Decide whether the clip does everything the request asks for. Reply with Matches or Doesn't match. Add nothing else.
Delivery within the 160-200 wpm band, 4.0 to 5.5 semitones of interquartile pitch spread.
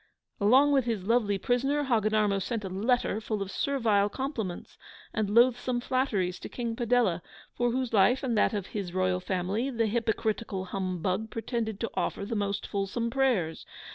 Doesn't match